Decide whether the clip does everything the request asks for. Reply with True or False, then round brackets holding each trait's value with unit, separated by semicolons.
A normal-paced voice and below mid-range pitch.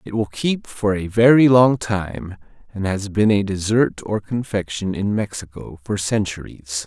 True (165 wpm; 100 Hz)